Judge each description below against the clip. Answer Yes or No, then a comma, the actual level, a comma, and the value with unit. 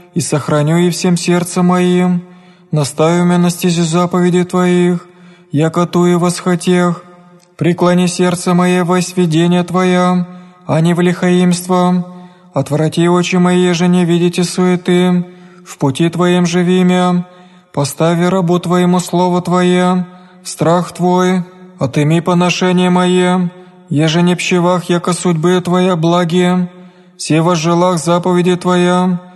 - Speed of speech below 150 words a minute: Yes, average, 125 wpm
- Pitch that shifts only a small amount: Yes, narrow, 0.6 semitones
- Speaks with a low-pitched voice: No, medium, 180 Hz